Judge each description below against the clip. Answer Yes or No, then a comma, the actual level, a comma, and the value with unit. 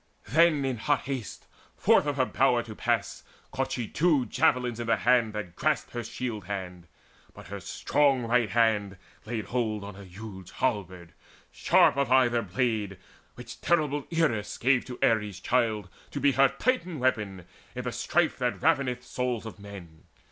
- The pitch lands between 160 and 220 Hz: No, low, 120 Hz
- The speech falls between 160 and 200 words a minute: Yes, average, 170 wpm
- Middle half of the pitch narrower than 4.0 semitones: No, average, 4.3 semitones